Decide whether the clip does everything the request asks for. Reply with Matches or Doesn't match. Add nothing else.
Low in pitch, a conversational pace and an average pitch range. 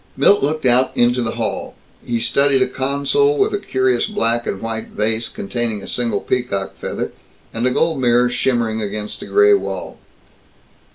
Matches